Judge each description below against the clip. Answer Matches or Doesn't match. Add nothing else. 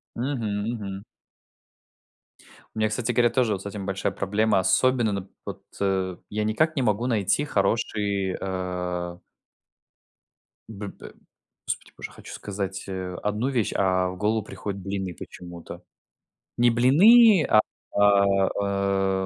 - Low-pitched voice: Matches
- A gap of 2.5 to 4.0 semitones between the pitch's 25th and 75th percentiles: Matches